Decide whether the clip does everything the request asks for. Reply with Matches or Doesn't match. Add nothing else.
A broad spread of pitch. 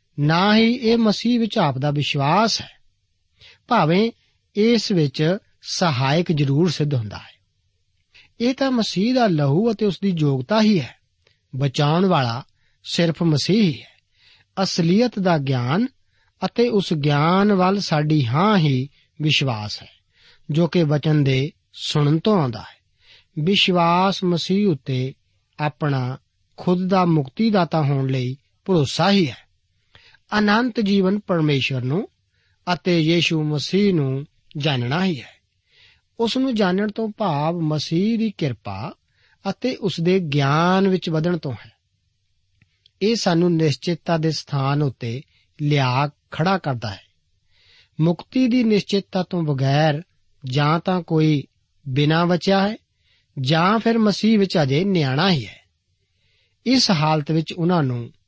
Matches